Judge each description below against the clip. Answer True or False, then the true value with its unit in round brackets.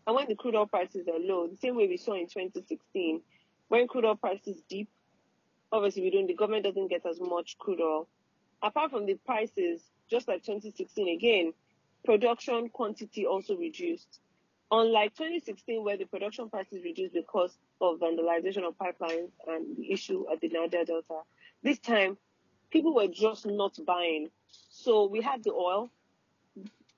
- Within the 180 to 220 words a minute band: False (165 wpm)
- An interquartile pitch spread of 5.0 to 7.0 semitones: True (5.4 semitones)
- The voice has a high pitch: True (205 Hz)